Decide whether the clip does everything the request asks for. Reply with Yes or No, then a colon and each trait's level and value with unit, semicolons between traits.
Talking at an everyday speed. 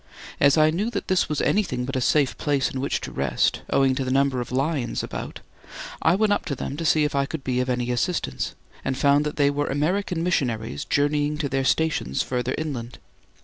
No: fast, 220 wpm